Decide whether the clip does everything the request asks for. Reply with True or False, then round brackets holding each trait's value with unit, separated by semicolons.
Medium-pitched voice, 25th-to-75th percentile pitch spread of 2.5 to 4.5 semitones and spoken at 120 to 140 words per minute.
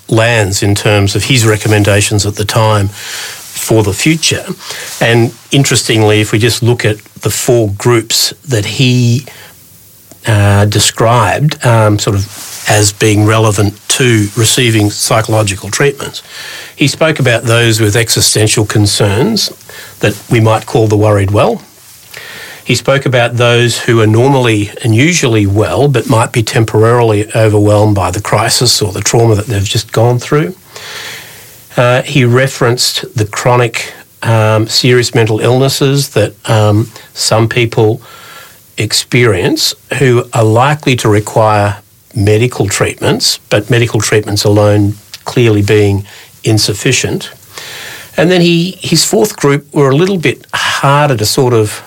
False (115 Hz; 3.3 semitones; 135 wpm)